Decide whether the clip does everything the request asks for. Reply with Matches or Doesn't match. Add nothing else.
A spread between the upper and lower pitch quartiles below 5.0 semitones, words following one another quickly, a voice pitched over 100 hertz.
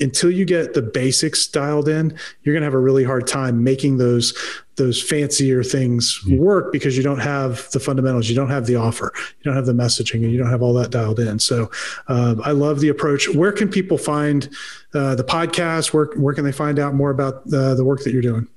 Matches